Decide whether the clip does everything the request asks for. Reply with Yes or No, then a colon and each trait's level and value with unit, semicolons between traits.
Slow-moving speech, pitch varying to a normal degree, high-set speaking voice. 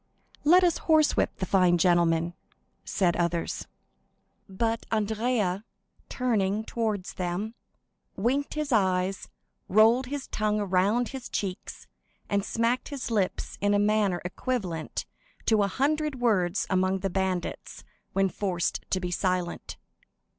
Yes: slow, 125 wpm; average, 4.3 semitones; high, 205 Hz